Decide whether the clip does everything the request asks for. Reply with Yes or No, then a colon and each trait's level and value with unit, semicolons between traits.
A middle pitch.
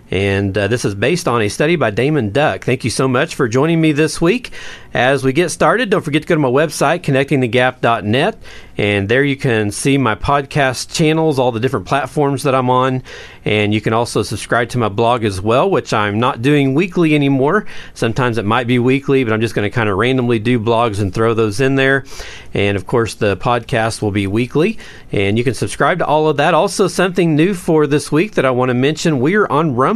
No: low, 130 Hz